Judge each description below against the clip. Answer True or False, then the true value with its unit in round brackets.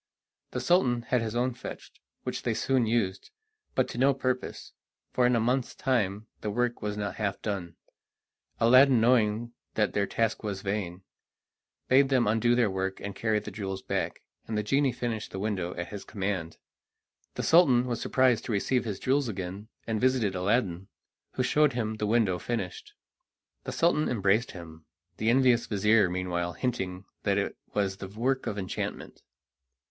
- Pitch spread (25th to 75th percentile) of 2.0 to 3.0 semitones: False (4.2 semitones)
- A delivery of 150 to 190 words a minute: True (170 wpm)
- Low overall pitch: True (110 Hz)